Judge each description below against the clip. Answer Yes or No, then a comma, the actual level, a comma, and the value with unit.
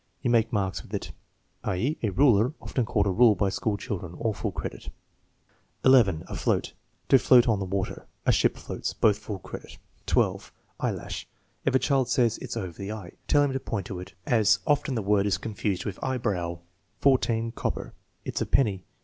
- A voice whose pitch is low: Yes, low, 110 Hz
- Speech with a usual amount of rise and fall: Yes, average, 4.2 semitones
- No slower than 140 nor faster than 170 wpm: No, average, 190 wpm